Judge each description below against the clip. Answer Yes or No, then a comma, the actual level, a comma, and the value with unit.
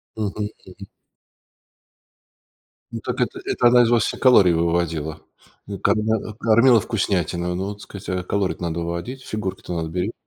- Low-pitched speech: Yes, very low, 95 Hz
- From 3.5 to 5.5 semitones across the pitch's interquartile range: Yes, average, 4.3 semitones